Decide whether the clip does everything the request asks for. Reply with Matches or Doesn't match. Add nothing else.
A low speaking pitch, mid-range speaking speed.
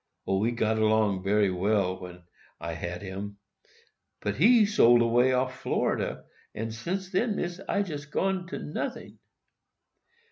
Matches